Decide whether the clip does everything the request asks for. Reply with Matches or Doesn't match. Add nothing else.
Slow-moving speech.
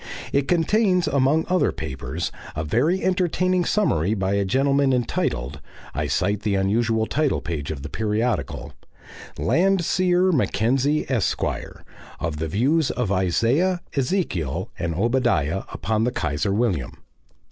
Matches